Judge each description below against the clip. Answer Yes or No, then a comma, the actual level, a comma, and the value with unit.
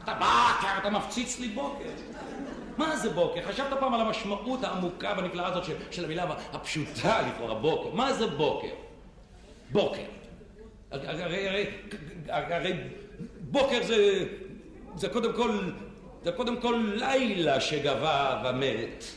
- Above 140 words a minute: No, average, 130 wpm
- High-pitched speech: Yes, high, 205 Hz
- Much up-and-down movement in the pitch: Yes, wide, 5.8 semitones